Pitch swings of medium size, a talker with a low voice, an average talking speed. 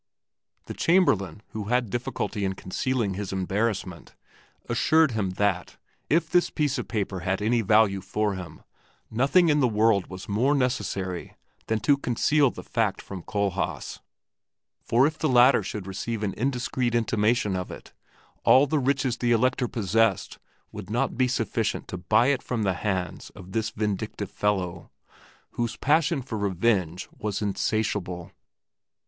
Yes: average, 4.4 semitones; low, 110 Hz; average, 150 wpm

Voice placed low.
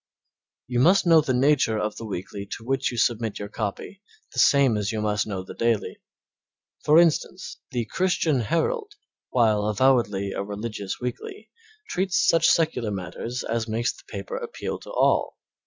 Yes: low, 120 Hz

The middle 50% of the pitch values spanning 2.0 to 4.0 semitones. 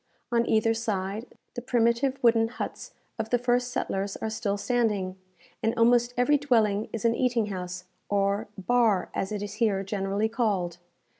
Yes: average, 3.2 semitones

